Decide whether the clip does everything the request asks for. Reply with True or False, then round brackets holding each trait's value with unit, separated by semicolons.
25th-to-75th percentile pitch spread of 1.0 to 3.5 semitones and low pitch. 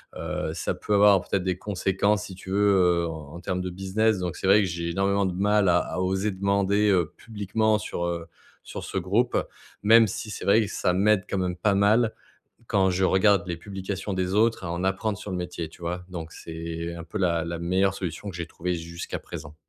True (2.8 semitones; 95 Hz)